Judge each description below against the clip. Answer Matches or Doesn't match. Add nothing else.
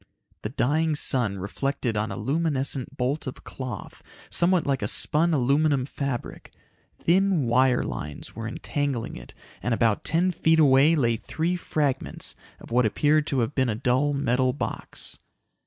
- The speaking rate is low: Doesn't match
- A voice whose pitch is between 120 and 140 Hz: Matches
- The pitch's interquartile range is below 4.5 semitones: Matches